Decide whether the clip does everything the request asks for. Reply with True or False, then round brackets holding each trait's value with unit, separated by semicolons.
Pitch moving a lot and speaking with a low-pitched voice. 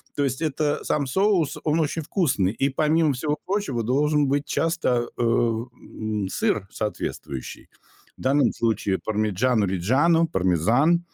True (6.0 semitones; 130 Hz)